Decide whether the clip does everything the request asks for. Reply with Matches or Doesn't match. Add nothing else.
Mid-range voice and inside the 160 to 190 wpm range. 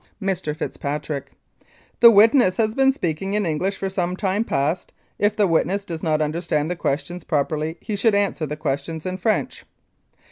Matches